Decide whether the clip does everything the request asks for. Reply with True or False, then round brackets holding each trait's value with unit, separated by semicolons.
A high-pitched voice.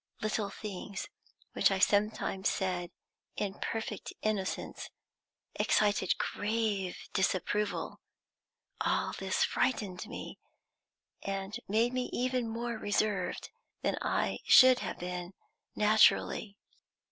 True (210 Hz)